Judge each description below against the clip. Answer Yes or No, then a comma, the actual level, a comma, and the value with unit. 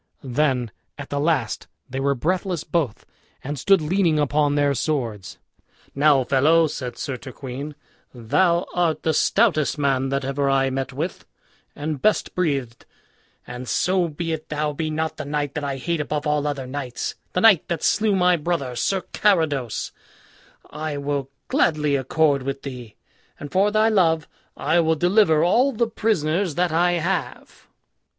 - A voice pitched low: No, medium, 150 Hz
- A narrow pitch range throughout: No, average, 3.9 semitones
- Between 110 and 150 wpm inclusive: No, average, 160 wpm